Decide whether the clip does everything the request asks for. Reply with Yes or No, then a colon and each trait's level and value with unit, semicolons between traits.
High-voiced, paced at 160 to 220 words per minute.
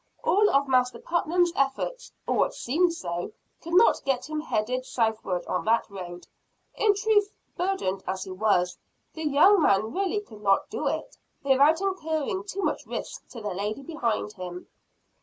Yes: very high, 275 Hz; average, 165 wpm